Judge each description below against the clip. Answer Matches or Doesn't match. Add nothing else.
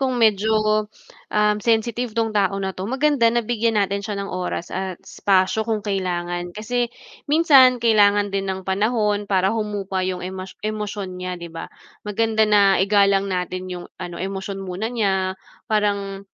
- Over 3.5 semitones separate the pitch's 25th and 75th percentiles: Doesn't match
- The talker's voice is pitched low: Doesn't match